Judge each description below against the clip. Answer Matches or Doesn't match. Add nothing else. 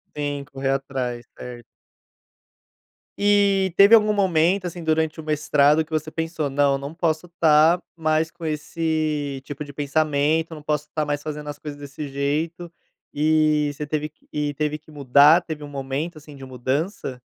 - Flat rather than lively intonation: Matches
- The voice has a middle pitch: Matches